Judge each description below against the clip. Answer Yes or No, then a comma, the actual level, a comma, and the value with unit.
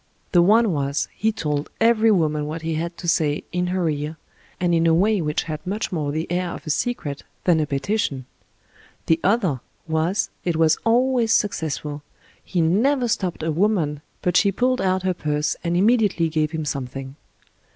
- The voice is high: No, medium, 170 Hz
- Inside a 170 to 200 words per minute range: Yes, average, 185 wpm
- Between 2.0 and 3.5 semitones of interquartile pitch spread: No, average, 4.8 semitones